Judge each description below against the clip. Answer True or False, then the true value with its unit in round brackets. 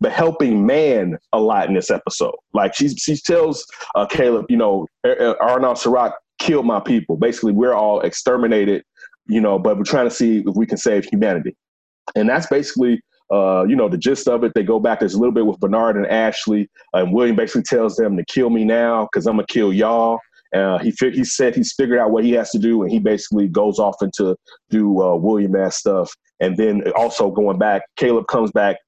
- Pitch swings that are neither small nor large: True (4.1 semitones)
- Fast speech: True (220 wpm)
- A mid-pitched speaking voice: False (115 Hz)